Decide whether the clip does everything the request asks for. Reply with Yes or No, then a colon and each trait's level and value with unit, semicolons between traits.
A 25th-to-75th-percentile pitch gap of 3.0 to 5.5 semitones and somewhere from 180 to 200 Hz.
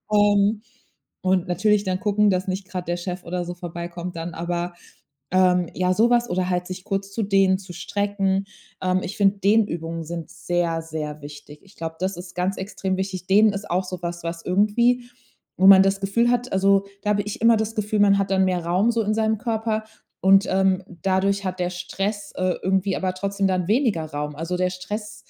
No: narrow, 2.4 semitones; high, 190 Hz